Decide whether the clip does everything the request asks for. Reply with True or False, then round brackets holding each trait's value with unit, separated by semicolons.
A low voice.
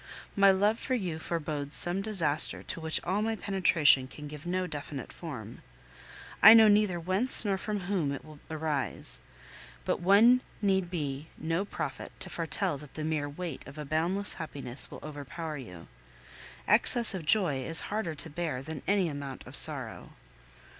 False (165 Hz)